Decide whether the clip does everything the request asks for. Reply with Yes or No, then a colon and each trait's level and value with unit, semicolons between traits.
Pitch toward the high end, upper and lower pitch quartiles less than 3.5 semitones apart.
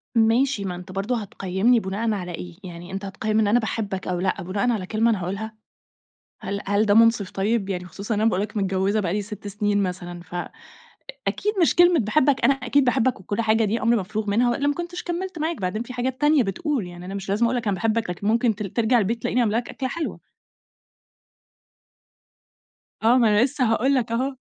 No: high, 215 Hz; average, 3.9 semitones